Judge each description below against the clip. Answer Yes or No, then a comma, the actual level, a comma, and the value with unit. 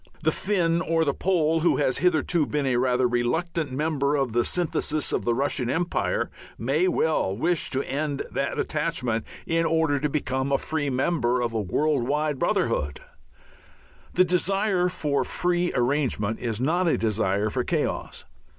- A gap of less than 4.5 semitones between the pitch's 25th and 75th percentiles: No, average, 4.8 semitones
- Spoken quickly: No, average, 160 wpm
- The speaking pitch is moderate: Yes, medium, 145 Hz